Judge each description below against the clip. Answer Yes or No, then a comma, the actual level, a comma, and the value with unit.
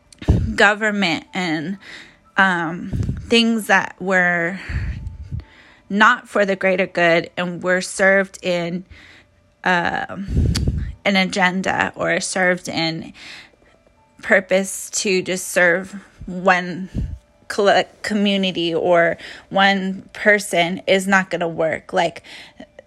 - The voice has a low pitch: No, high, 190 Hz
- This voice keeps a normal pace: No, slow, 95 wpm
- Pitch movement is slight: Yes, narrow, 1.8 semitones